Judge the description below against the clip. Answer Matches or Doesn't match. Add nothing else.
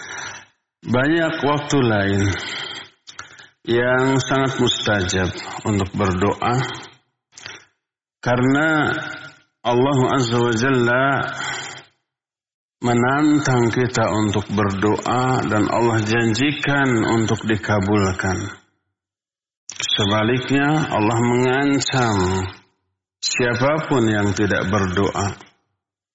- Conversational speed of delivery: Doesn't match